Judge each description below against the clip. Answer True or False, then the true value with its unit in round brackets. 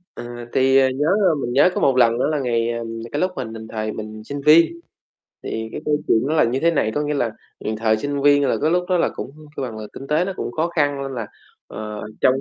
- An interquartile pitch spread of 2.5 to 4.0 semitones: False (4.5 semitones)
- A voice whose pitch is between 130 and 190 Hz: True (135 Hz)